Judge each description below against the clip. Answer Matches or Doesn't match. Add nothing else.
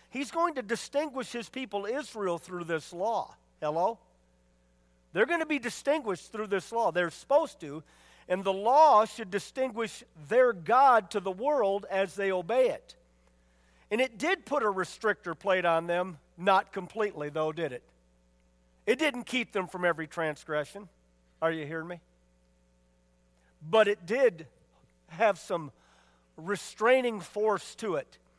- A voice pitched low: Doesn't match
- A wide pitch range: Matches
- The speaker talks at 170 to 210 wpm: Doesn't match